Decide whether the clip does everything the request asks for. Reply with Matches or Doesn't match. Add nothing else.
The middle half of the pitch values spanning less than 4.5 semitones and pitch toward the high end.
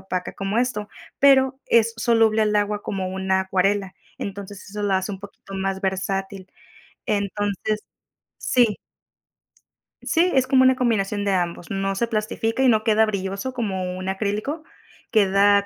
Matches